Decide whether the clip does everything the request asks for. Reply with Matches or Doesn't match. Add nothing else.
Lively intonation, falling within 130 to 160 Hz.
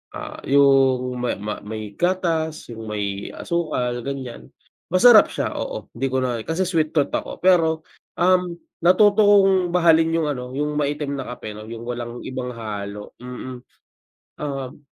Matches